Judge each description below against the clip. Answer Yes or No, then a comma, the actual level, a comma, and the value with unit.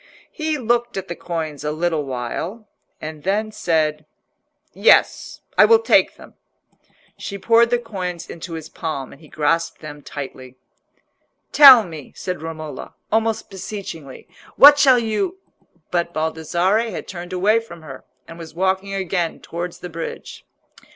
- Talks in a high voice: No, medium, 175 Hz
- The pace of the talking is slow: No, average, 145 wpm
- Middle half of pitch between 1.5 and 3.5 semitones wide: No, wide, 5.4 semitones